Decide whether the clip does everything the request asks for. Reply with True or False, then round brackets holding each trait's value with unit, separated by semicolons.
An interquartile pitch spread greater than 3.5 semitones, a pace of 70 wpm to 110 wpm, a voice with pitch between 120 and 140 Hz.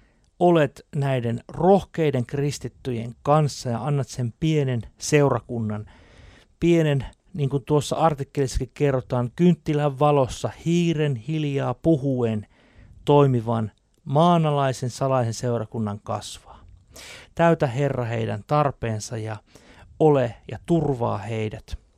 True (4.7 semitones; 95 wpm; 130 Hz)